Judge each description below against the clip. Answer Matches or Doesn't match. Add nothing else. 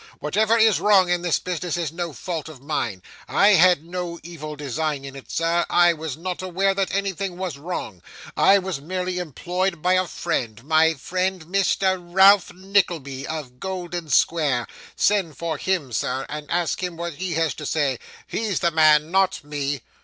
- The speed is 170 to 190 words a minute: Matches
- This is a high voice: Doesn't match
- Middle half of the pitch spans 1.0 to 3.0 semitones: Doesn't match